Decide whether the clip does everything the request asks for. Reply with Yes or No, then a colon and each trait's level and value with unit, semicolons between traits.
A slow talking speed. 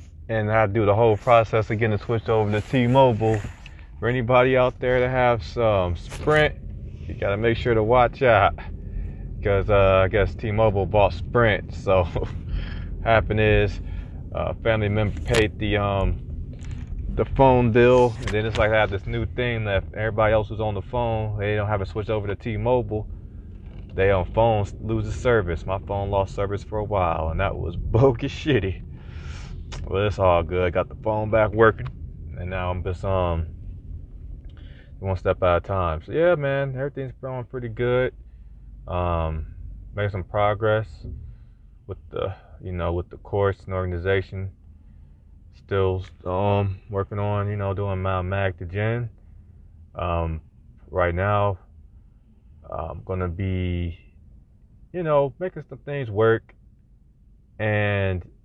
No: average, 160 wpm